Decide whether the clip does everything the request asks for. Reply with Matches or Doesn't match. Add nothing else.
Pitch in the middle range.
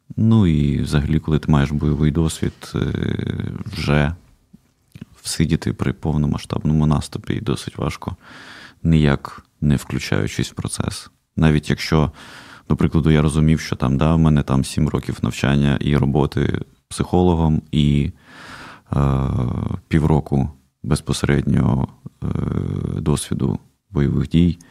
Doesn't match